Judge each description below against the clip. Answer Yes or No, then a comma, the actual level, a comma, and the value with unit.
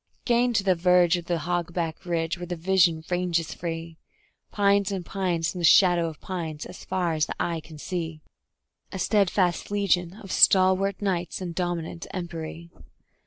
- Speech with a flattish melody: Yes, narrow, 2.1 semitones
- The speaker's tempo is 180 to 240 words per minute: No, average, 170 wpm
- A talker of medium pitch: Yes, medium, 175 Hz